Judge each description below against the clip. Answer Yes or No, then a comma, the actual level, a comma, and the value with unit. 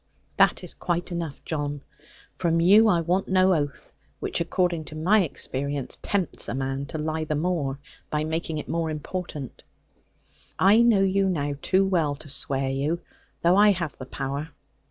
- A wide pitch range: No, average, 4.2 semitones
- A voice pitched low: No, medium, 160 Hz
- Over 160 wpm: Yes, average, 170 wpm